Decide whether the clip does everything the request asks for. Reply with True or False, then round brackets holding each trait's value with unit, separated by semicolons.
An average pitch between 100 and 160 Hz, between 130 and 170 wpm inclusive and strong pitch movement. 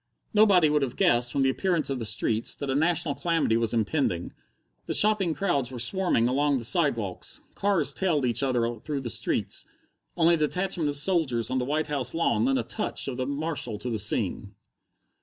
False (140 Hz; 195 wpm; 5.9 semitones)